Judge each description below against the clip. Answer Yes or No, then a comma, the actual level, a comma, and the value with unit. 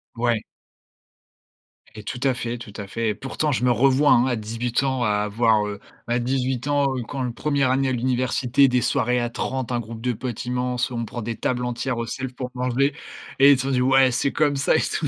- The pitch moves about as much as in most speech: No, narrow, 2.1 semitones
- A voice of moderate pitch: No, low, 125 Hz